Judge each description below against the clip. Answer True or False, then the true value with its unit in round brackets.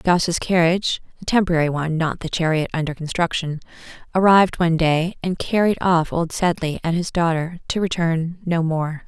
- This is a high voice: False (170 Hz)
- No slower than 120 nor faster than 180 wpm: True (160 wpm)